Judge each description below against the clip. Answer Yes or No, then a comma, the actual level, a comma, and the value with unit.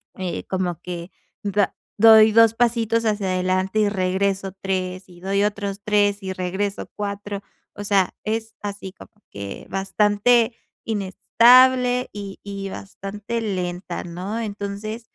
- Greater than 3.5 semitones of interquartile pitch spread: No, narrow, 2.4 semitones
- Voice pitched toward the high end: Yes, high, 200 Hz